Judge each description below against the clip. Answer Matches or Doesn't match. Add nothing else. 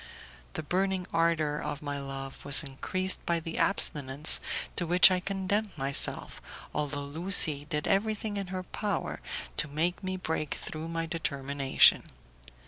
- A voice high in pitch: Doesn't match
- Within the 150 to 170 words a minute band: Doesn't match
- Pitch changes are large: Doesn't match